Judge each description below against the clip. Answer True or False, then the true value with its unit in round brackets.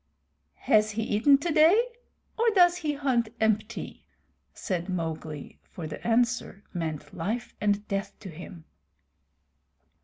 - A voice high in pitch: True (215 Hz)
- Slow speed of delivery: True (120 wpm)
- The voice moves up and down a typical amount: False (7.3 semitones)